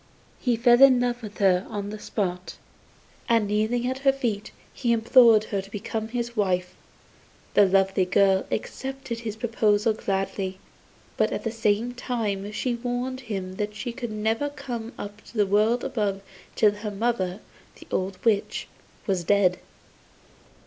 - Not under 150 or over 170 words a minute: Yes, average, 155 wpm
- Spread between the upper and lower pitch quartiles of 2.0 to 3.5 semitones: Yes, average, 3.1 semitones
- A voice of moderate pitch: No, high, 215 Hz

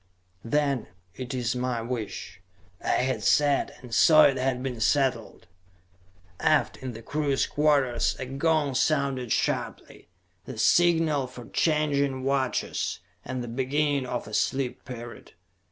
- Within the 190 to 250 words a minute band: No, slow, 135 wpm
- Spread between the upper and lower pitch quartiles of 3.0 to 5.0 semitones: No, narrow, 2.6 semitones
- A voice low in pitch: Yes, low, 130 Hz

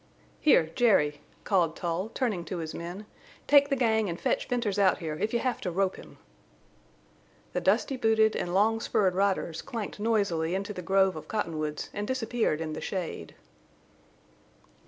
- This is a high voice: Yes, high, 195 Hz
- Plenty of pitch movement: No, average, 4.8 semitones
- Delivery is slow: No, average, 165 wpm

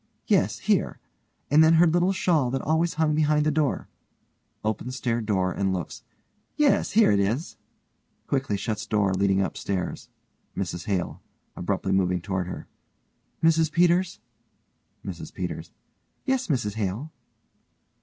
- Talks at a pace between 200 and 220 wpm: No, slow, 135 wpm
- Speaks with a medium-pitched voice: No, low, 120 Hz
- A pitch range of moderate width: No, wide, 8.5 semitones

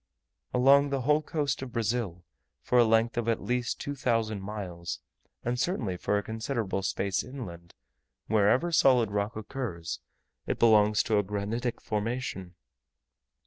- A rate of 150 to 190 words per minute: No, average, 140 wpm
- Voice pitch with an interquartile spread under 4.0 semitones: Yes, average, 3.6 semitones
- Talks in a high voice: No, low, 115 Hz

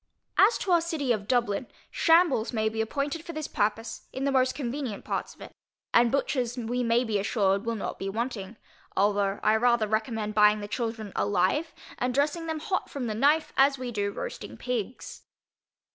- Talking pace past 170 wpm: Yes, average, 190 wpm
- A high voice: Yes, high, 240 Hz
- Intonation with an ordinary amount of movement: Yes, average, 4.6 semitones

